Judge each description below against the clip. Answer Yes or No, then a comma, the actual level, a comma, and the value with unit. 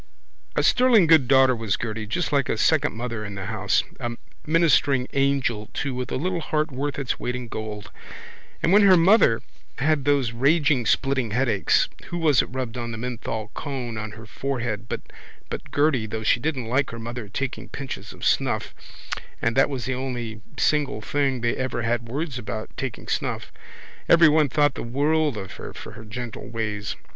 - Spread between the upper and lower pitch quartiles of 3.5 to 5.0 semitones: Yes, average, 4.1 semitones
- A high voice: No, low, 125 Hz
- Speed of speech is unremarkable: Yes, average, 180 wpm